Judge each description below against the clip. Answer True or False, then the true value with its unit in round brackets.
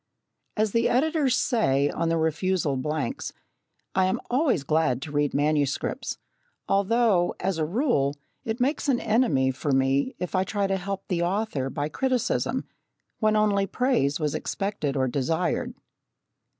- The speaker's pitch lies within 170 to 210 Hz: True (185 Hz)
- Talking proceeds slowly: False (150 wpm)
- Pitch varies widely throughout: True (7.3 semitones)